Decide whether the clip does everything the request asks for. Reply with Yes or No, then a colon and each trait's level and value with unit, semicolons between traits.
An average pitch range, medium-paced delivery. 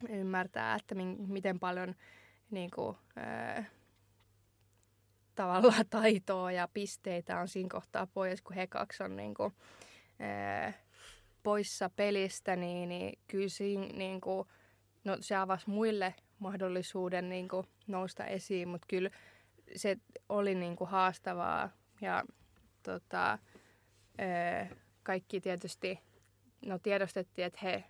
No: narrow, 1.9 semitones; average, 120 wpm